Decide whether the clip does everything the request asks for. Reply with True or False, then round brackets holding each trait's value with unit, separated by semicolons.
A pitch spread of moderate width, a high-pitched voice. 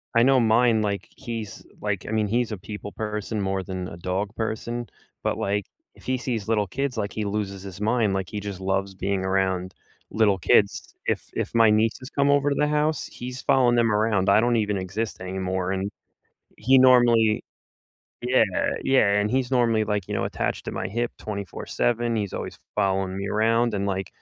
False (3.4 semitones; 105 Hz)